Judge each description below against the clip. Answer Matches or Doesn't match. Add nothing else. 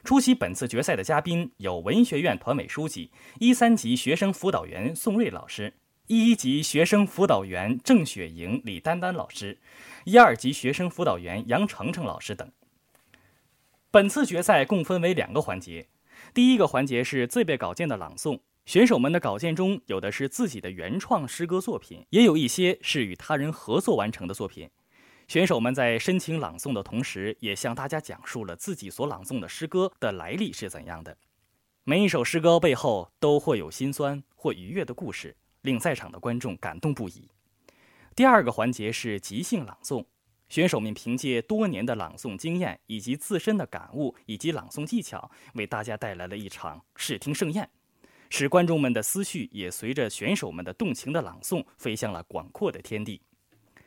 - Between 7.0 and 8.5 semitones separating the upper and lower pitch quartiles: Matches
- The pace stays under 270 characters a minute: Doesn't match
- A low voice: Doesn't match